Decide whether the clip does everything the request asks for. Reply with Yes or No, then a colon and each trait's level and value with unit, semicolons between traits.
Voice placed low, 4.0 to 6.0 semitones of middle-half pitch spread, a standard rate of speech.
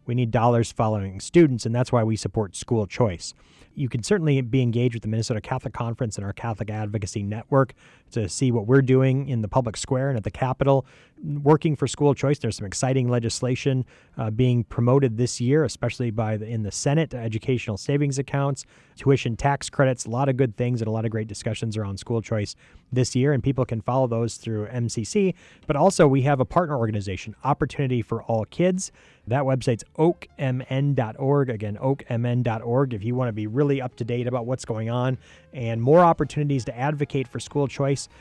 No: low, 125 Hz; average, 3.3 semitones; average, 195 wpm